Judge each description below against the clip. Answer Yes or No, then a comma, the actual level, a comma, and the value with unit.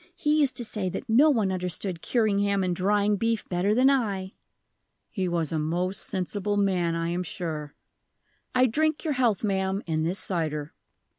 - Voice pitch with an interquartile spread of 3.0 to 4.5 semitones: Yes, average, 4.1 semitones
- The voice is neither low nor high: No, high, 195 Hz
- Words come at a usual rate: Yes, average, 175 wpm